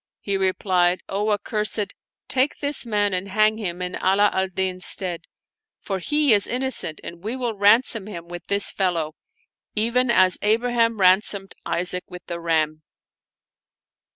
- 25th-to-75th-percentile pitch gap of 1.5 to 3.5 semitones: Yes, average, 3.2 semitones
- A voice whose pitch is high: Yes, high, 200 Hz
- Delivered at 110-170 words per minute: Yes, average, 155 wpm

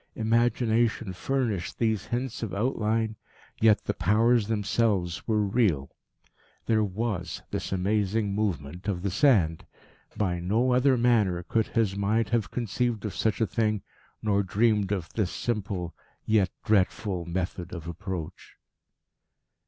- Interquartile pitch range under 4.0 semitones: Yes, average, 3.4 semitones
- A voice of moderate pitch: No, low, 105 Hz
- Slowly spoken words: Yes, slow, 130 wpm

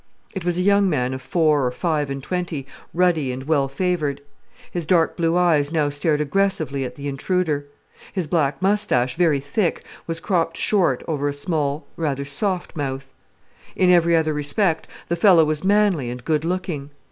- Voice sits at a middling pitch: Yes, medium, 155 Hz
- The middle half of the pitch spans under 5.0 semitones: Yes, average, 4.0 semitones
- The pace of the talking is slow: No, average, 175 wpm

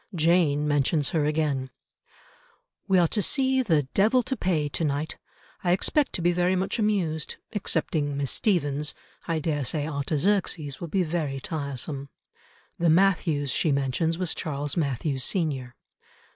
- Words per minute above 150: No, average, 145 wpm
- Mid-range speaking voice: Yes, medium, 160 Hz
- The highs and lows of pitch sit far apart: No, average, 3.9 semitones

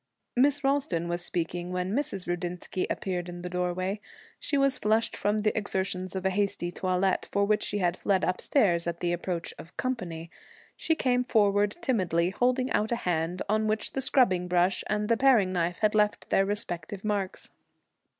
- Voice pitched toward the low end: No, high, 195 Hz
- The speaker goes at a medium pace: Yes, average, 180 wpm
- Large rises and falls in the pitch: No, average, 3.5 semitones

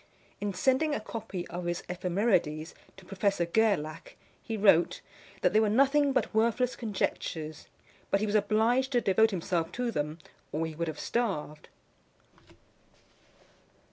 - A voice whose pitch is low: No, high, 205 Hz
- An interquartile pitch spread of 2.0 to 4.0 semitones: No, average, 5.2 semitones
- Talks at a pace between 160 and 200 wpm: No, average, 140 wpm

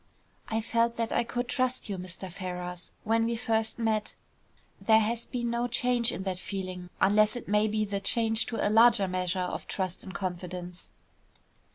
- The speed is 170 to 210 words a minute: Yes, average, 180 wpm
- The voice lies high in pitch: Yes, high, 215 Hz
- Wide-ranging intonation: No, average, 3.8 semitones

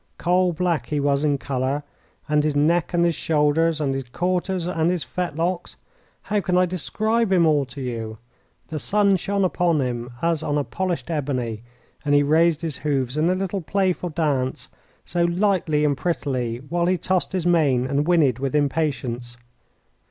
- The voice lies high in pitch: No, medium, 155 Hz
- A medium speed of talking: Yes, average, 175 wpm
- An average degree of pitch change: Yes, average, 4.2 semitones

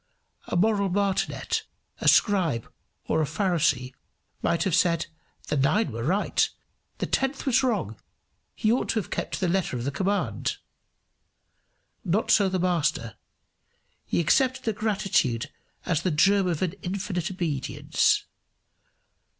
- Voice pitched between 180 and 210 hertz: Yes, medium, 185 Hz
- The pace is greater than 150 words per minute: No, average, 140 wpm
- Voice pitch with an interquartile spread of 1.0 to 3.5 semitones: No, average, 4.8 semitones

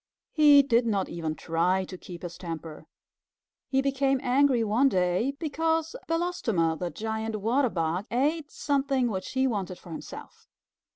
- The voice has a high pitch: Yes, high, 230 Hz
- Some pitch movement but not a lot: No, wide, 7.4 semitones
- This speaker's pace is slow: No, average, 150 wpm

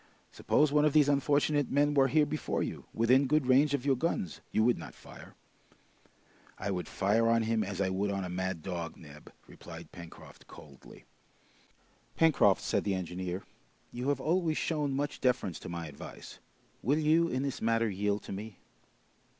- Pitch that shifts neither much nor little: No, wide, 7.4 semitones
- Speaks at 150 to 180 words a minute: Yes, average, 175 wpm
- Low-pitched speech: Yes, low, 115 Hz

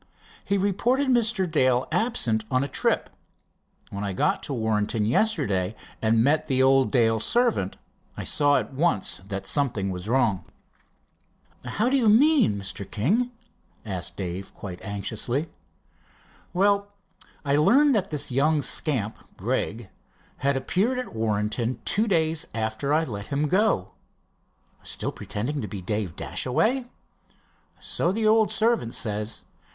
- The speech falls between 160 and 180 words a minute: No, average, 140 wpm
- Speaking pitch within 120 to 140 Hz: Yes, low, 135 Hz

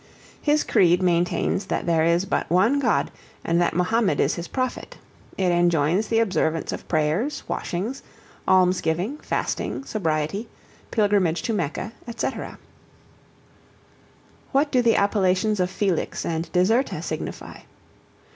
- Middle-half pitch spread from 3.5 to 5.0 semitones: Yes, average, 4.6 semitones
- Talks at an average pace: No, slow, 125 wpm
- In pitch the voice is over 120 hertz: Yes, medium, 185 Hz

